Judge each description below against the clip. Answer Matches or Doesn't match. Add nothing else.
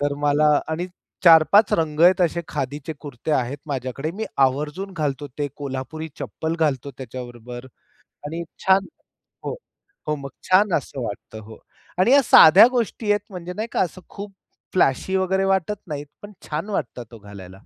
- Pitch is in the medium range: Matches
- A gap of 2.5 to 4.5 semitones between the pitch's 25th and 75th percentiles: Doesn't match